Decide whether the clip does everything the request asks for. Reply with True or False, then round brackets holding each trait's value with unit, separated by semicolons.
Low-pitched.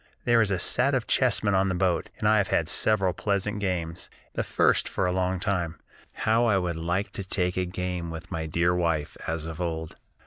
True (90 Hz)